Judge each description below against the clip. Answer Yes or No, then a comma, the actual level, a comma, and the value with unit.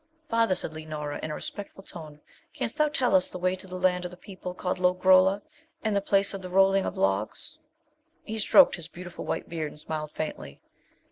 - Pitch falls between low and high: Yes, medium, 180 Hz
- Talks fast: Yes, fast, 210 wpm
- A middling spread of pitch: Yes, average, 3.7 semitones